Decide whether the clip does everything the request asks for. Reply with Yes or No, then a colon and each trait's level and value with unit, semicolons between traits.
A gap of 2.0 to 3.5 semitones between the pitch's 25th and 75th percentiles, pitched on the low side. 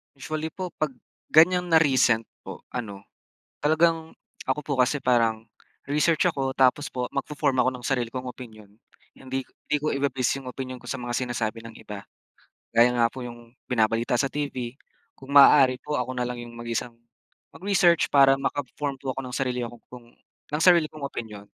Yes: average, 3.2 semitones; low, 130 Hz